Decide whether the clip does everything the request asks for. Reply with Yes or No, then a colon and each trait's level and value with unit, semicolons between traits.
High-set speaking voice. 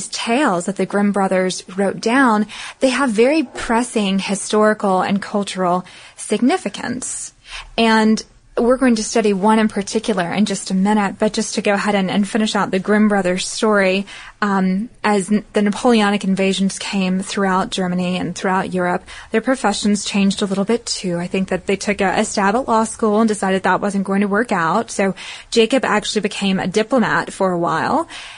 Yes: high, 205 Hz